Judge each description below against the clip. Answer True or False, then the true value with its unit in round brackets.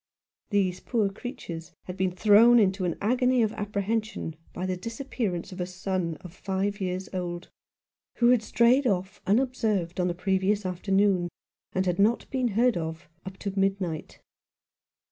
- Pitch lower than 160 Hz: False (195 Hz)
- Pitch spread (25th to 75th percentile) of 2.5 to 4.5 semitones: True (3.3 semitones)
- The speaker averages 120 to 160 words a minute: True (155 wpm)